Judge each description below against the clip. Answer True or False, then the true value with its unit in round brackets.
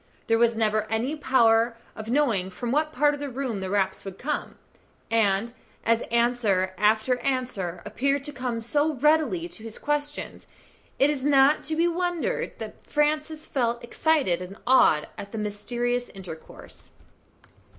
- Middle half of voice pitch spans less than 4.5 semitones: False (5.3 semitones)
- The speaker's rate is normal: True (160 wpm)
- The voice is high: True (240 Hz)